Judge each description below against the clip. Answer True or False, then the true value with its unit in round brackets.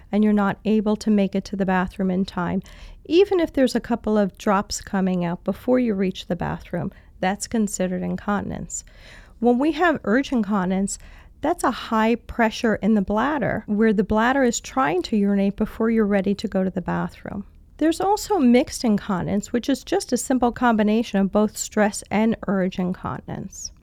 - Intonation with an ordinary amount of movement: True (3.8 semitones)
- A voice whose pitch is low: False (215 Hz)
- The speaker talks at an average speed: True (180 wpm)